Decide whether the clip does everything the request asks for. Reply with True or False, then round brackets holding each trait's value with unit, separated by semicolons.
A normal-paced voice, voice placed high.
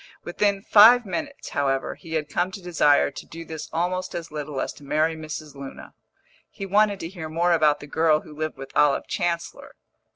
False (195 wpm; 160 Hz)